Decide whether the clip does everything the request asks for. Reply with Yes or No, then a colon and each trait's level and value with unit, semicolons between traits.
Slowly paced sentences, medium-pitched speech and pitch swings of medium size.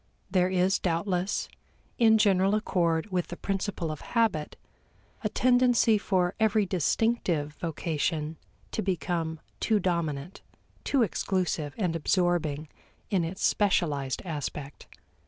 Yes: slow, 115 wpm; medium, 180 Hz; average, 3.9 semitones